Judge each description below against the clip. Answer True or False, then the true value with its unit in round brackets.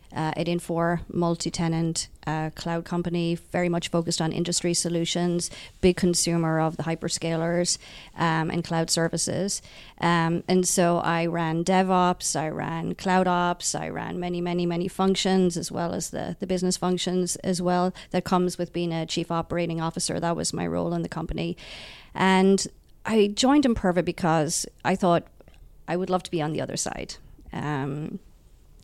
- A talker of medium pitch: True (175 Hz)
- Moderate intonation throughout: False (1.5 semitones)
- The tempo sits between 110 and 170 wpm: True (165 wpm)